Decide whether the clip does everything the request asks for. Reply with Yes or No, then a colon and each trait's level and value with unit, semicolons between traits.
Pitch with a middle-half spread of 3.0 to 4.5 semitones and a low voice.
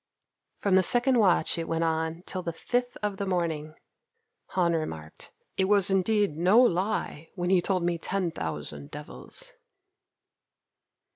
No: average, 3.5 semitones; medium, 175 Hz